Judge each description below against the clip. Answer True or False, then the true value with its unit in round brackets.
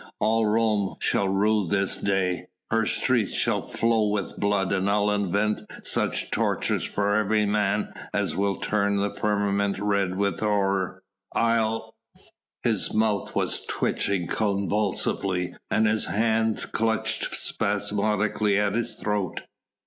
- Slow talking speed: True (125 wpm)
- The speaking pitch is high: False (105 Hz)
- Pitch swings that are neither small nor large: False (1.6 semitones)